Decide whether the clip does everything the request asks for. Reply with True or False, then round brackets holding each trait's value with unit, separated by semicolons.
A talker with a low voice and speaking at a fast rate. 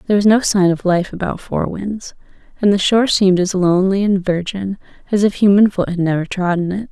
False (190 Hz; 215 wpm)